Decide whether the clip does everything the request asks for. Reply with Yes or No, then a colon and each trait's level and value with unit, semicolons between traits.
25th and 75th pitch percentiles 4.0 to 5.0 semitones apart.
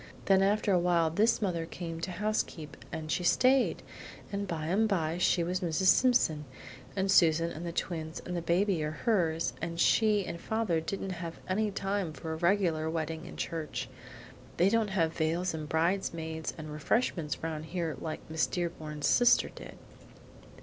No: average, 3.3 semitones